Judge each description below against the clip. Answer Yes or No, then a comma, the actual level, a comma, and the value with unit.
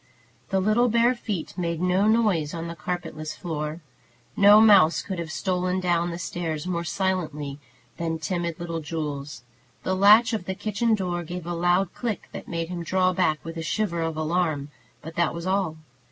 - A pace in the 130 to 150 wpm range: No, average, 180 wpm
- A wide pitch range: No, narrow, 2.6 semitones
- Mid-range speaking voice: Yes, medium, 175 Hz